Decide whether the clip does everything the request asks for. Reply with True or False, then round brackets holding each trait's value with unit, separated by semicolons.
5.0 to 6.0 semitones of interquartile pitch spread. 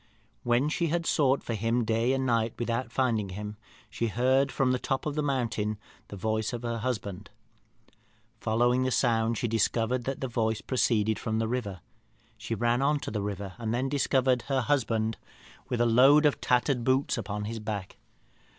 False (2.8 semitones)